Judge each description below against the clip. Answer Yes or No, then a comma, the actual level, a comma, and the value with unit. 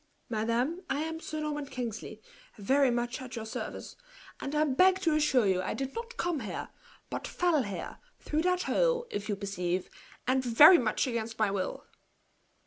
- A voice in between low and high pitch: No, very high, 260 Hz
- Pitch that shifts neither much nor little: No, wide, 6.0 semitones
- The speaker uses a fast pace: No, average, 175 wpm